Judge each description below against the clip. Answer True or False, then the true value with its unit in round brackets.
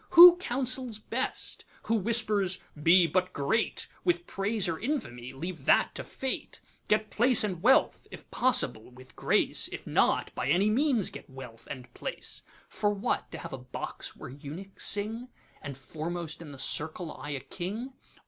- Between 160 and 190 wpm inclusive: False (145 wpm)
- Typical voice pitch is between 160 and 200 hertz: True (190 Hz)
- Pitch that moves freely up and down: True (8.0 semitones)